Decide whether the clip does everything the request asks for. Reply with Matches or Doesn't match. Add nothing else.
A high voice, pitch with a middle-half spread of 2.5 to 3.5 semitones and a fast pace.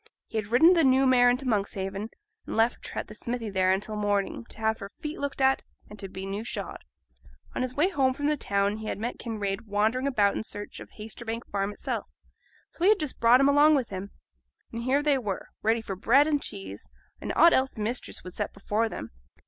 Doesn't match